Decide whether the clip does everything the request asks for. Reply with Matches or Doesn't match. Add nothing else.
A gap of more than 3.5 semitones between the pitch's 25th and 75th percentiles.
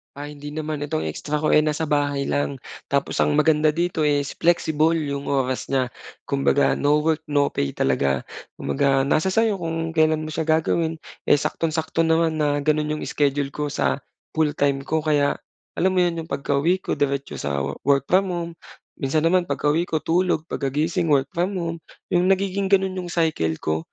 Doesn't match